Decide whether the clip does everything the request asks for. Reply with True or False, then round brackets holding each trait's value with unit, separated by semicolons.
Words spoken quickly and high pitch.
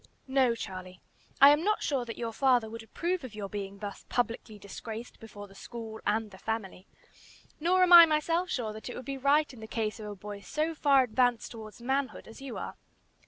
True (210 wpm; 230 Hz)